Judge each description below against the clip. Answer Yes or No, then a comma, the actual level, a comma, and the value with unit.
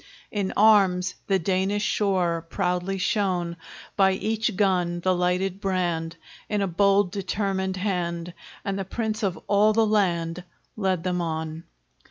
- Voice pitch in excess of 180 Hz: Yes, high, 190 Hz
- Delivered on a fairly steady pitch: Yes, narrow, 2.2 semitones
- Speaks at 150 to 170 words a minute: No, average, 140 wpm